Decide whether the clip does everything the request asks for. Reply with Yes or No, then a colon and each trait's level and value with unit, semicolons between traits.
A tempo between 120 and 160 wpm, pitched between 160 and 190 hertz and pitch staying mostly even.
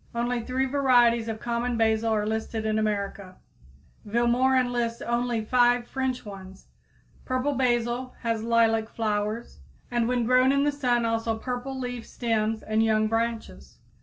No: average, 145 wpm; high, 235 Hz; narrow, 2.0 semitones